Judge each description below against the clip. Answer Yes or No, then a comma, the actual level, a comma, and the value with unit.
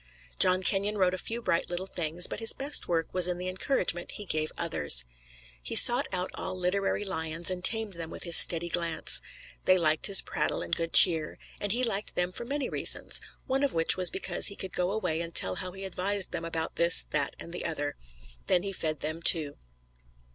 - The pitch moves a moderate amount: Yes, average, 3.0 semitones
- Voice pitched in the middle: Yes, medium, 180 Hz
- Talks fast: Yes, fast, 210 wpm